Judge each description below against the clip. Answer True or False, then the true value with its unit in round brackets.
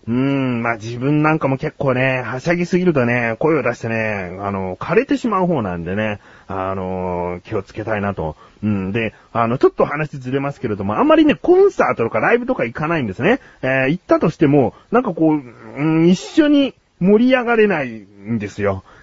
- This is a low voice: True (130 Hz)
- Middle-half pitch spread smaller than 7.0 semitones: False (8.4 semitones)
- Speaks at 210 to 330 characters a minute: False (390 characters per minute)